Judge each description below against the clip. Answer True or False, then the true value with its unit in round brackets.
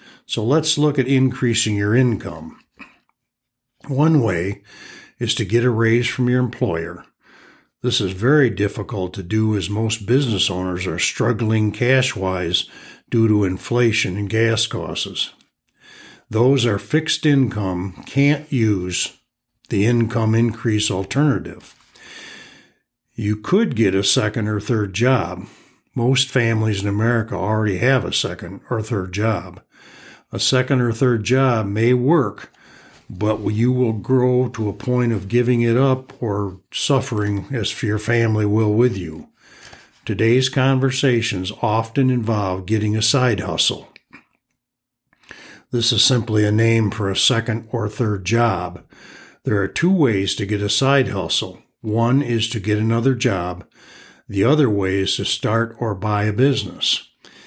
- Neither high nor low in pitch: False (115 Hz)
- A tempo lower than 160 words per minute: True (140 wpm)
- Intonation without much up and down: False (3.6 semitones)